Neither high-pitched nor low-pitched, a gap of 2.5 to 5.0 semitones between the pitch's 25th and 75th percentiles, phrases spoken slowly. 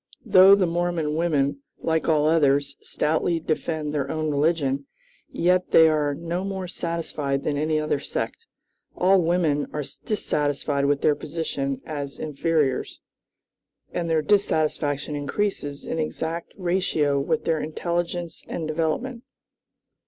Yes: medium, 155 Hz; average, 3.1 semitones; slow, 130 wpm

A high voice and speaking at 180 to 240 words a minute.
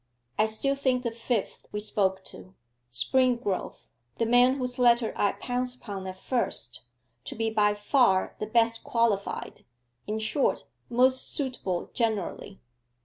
No: high, 230 Hz; average, 140 wpm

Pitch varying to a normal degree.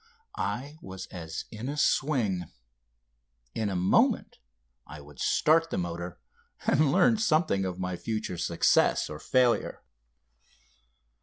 No: wide, 8.4 semitones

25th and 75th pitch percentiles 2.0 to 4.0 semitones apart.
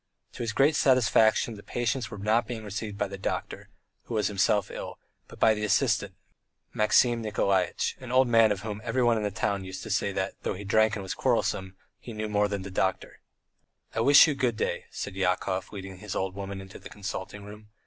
Yes: average, 2.7 semitones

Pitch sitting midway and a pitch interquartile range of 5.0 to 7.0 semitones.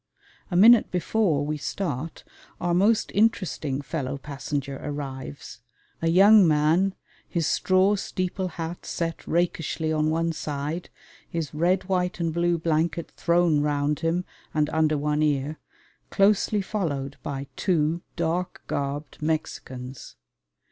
No: medium, 160 Hz; average, 3.4 semitones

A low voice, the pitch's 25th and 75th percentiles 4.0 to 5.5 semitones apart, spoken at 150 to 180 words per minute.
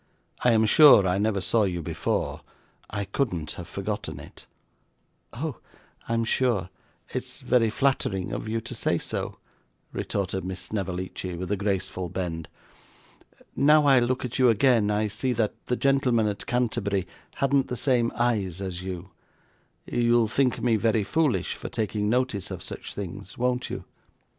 Yes: low, 110 Hz; average, 4.5 semitones; average, 155 wpm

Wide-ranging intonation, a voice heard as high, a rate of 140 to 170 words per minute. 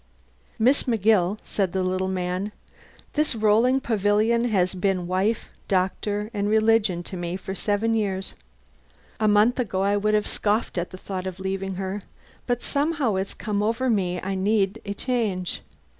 No: average, 2.9 semitones; high, 205 Hz; average, 160 wpm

